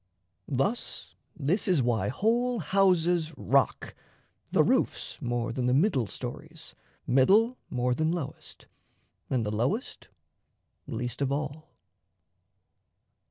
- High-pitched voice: No, medium, 145 Hz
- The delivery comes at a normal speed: No, slow, 110 wpm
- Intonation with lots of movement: Yes, wide, 6.6 semitones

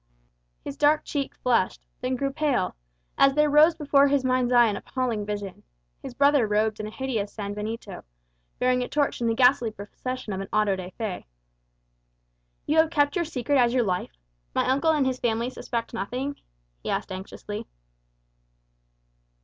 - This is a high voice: Yes, very high, 250 Hz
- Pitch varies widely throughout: No, average, 4.8 semitones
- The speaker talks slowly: No, average, 165 wpm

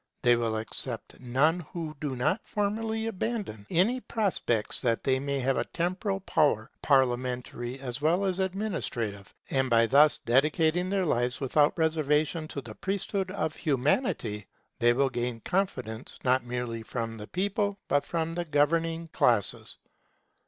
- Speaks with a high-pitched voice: No, medium, 145 Hz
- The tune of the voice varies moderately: No, wide, 6.6 semitones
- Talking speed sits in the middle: Yes, average, 145 wpm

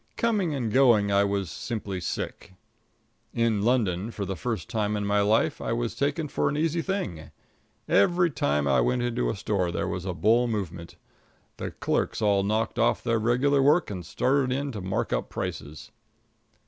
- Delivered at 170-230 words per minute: Yes, average, 180 wpm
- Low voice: Yes, low, 110 Hz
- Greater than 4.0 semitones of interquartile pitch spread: Yes, average, 4.8 semitones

